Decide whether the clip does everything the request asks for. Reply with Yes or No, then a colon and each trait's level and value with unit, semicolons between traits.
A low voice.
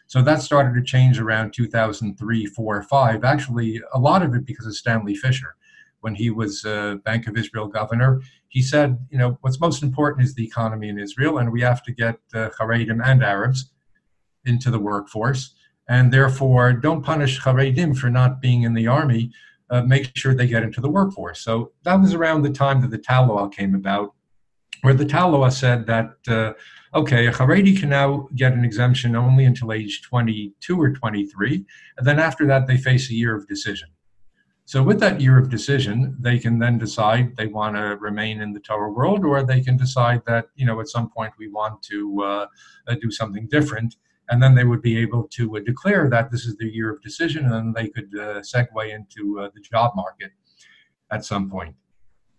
Yes: low, 120 Hz